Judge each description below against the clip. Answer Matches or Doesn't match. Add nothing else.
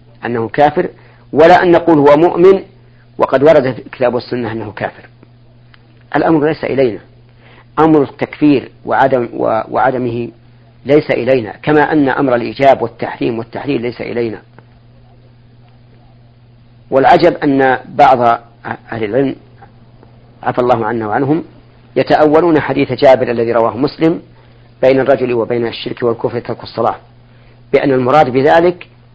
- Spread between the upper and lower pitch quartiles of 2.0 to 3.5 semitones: Matches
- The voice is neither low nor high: Doesn't match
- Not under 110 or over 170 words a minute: Matches